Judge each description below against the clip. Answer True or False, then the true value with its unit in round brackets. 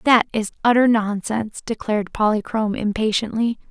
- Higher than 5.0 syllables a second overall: True (5.5 syllables/s)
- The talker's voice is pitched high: True (220 Hz)